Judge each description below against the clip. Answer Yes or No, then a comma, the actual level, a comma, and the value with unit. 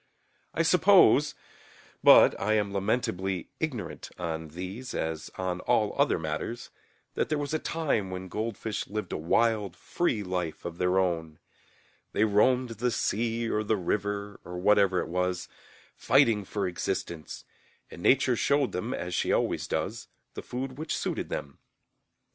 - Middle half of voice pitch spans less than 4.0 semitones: No, average, 4.5 semitones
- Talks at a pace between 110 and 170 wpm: Yes, average, 150 wpm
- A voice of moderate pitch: No, low, 100 Hz